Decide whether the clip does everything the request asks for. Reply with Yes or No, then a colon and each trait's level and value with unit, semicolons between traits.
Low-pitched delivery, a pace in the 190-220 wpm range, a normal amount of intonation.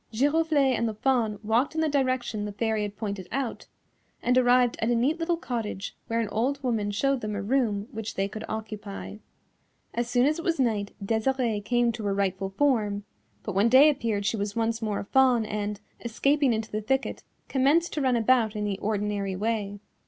No: high, 225 Hz; average, 200 wpm; average, 3.9 semitones